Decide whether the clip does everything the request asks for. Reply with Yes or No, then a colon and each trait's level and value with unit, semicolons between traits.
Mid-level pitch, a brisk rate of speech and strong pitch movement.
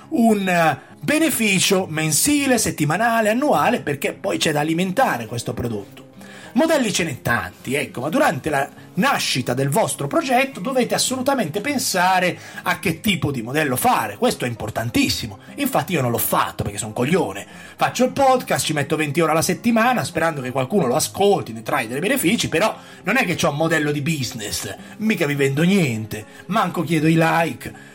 Yes: medium, 165 Hz; fast, 175 wpm; wide, 8.3 semitones